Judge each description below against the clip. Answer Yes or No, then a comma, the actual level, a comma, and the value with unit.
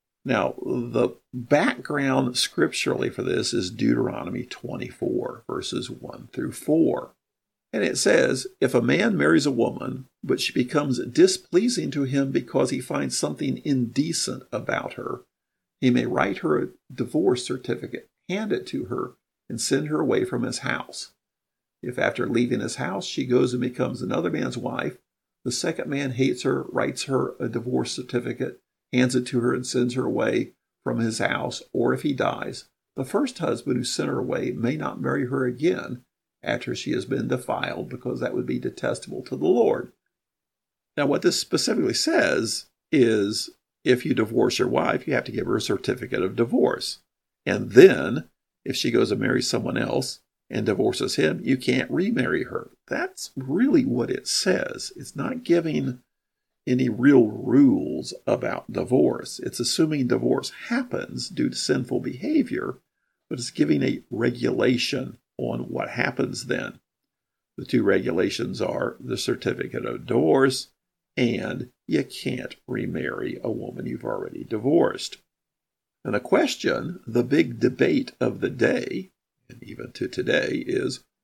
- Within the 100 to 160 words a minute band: Yes, average, 155 wpm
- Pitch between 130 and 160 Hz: Yes, low, 135 Hz